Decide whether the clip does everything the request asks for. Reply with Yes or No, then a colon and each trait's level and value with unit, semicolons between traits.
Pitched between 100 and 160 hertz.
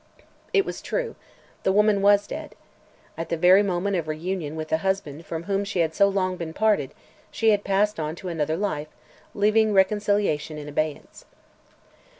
No: high, 190 Hz